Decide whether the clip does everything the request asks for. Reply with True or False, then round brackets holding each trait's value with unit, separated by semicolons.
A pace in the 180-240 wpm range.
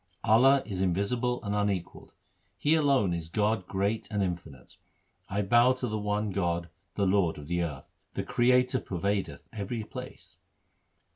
False (150 wpm)